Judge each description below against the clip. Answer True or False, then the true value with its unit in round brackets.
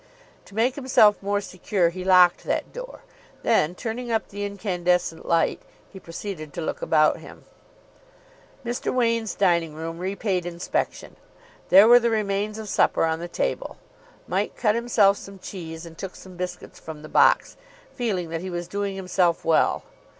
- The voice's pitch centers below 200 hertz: True (190 Hz)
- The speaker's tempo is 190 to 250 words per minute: False (165 wpm)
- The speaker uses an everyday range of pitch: True (3.7 semitones)